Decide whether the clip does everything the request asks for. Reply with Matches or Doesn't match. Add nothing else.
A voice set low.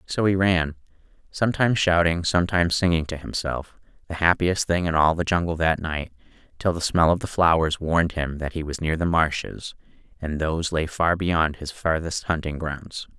Matches